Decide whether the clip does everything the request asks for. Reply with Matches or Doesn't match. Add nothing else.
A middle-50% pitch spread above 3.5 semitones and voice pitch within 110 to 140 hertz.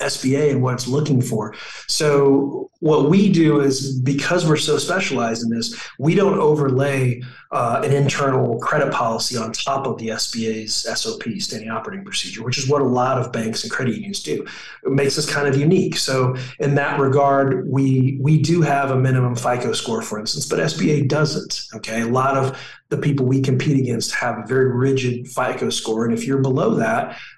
Doesn't match